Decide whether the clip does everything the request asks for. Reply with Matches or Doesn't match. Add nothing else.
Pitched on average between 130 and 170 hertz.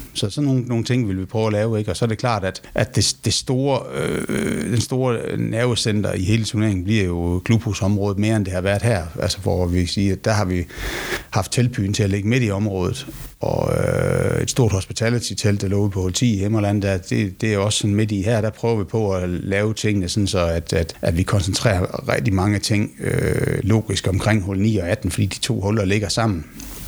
Doesn't match